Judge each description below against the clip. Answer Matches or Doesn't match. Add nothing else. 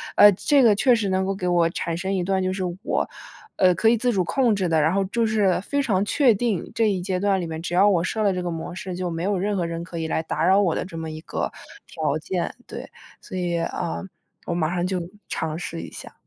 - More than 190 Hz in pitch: Doesn't match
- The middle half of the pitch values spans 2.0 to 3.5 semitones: Matches